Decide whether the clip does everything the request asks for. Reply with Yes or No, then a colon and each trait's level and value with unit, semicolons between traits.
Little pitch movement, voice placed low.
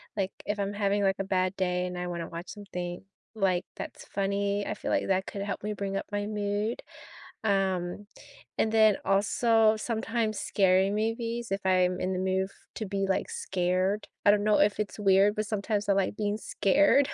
No: narrow, 1.9 semitones; high, 200 Hz